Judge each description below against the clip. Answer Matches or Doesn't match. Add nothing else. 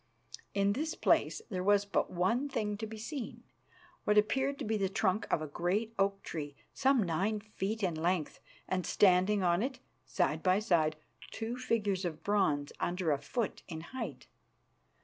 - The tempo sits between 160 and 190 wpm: Matches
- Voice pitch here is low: Doesn't match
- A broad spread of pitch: Doesn't match